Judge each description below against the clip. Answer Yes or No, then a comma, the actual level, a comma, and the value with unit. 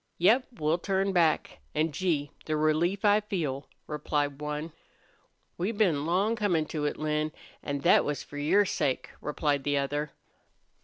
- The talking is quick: No, average, 155 wpm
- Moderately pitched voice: Yes, medium, 155 Hz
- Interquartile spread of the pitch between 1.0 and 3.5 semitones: No, average, 4.2 semitones